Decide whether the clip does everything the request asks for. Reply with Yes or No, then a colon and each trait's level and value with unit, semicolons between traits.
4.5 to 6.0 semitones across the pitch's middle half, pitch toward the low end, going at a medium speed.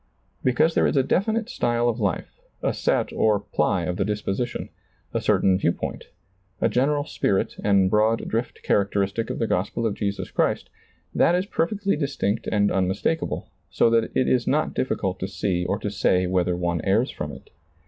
Yes: average, 4.9 semitones; low, 105 Hz; average, 190 wpm